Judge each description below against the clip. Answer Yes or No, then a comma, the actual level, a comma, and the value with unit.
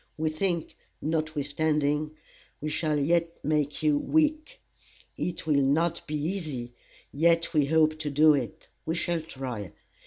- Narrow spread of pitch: Yes, narrow, 2.2 semitones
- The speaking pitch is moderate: Yes, medium, 155 Hz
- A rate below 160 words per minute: Yes, slow, 135 wpm